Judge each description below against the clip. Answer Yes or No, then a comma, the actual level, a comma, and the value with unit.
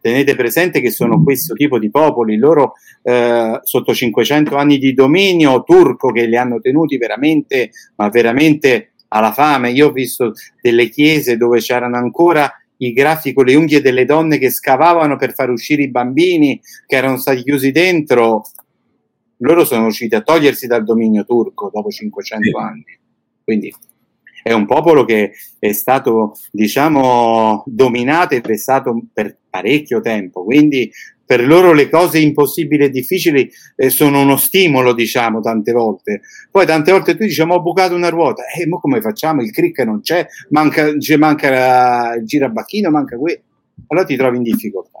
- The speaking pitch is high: No, medium, 140 Hz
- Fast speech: No, average, 160 wpm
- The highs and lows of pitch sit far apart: No, average, 5.0 semitones